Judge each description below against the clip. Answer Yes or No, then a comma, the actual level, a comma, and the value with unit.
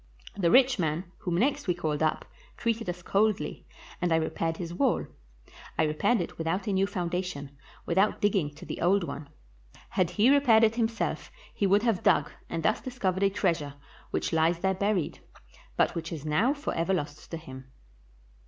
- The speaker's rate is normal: Yes, average, 180 wpm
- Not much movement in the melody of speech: No, average, 4.3 semitones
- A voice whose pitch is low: No, medium, 180 Hz